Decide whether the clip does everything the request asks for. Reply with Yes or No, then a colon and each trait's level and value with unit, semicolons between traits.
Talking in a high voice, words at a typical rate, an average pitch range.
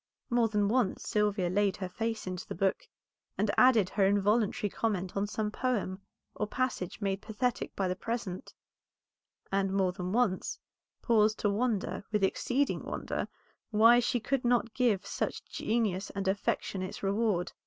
Yes: high, 210 Hz; average, 155 wpm; average, 3.1 semitones